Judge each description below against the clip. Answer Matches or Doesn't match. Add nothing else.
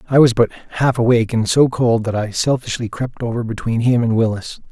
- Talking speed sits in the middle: Doesn't match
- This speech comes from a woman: Doesn't match